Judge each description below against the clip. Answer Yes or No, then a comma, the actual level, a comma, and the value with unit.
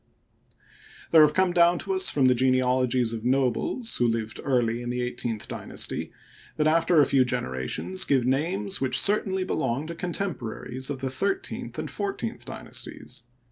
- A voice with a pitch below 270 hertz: Yes, low, 135 Hz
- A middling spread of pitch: No, wide, 6.6 semitones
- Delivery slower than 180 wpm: Yes, average, 155 wpm